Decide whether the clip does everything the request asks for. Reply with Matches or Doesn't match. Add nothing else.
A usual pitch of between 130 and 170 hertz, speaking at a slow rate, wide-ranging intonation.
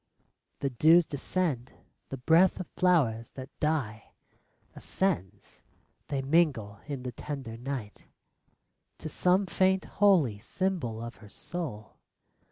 Matches